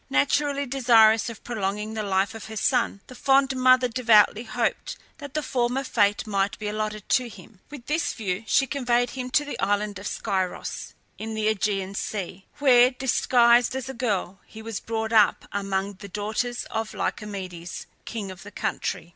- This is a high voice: Yes, high, 220 Hz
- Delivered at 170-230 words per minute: Yes, average, 175 wpm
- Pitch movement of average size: Yes, average, 3.7 semitones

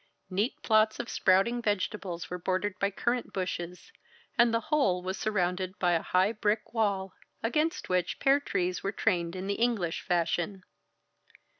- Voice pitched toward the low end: No, high, 195 Hz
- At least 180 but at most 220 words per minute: No, average, 155 wpm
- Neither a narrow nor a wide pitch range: Yes, average, 3.6 semitones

